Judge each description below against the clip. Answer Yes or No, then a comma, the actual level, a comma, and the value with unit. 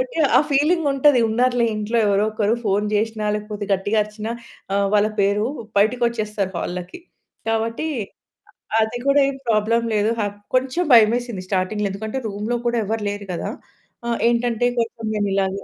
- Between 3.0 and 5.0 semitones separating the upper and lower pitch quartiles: No, narrow, 2.6 semitones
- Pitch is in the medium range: No, high, 220 Hz